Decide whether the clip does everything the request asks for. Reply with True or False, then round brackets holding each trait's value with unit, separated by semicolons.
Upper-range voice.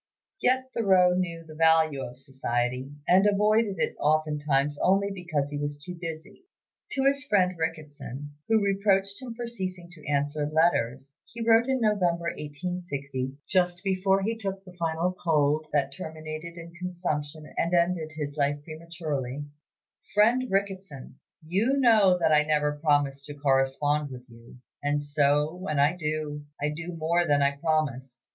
False (160 Hz)